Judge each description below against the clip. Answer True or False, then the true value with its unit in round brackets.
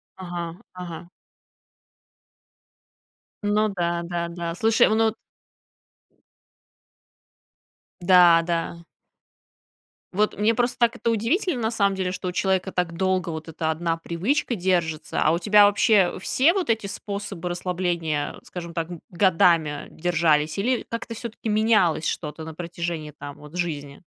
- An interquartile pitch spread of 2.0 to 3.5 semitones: False (3.9 semitones)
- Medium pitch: True (180 Hz)